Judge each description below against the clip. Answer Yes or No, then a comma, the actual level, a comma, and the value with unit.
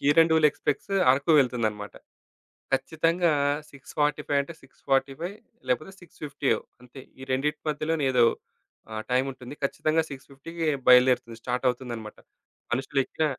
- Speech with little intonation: No, average, 3.6 semitones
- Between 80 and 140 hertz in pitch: Yes, low, 135 Hz